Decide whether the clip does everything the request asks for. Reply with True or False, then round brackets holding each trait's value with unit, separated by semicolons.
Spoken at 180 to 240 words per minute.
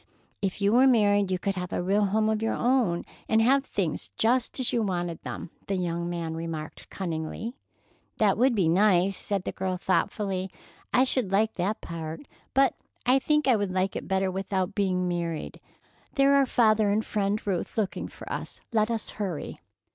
True (185 wpm)